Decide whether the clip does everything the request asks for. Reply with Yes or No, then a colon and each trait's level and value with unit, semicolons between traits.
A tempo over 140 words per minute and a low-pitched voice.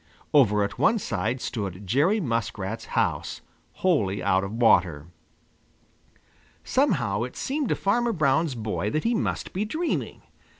No: slow, 135 wpm; low, 120 Hz